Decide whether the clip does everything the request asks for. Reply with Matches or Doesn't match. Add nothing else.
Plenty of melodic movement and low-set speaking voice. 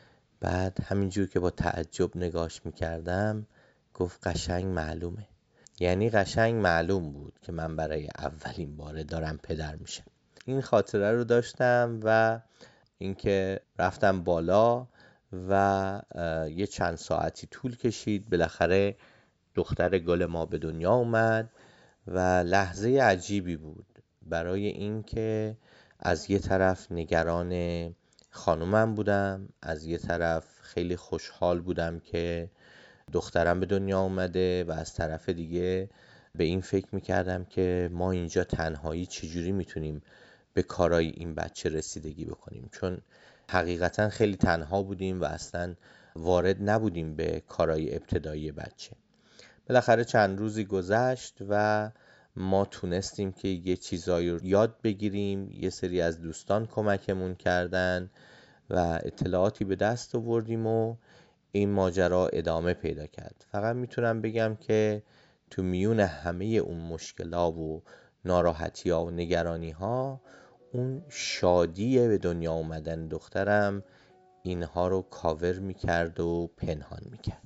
Doesn't match